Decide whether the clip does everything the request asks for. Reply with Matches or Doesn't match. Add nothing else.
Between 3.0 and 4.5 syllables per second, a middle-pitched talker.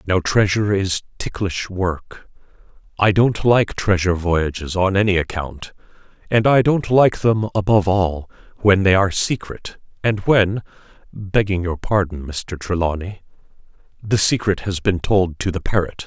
Doesn't match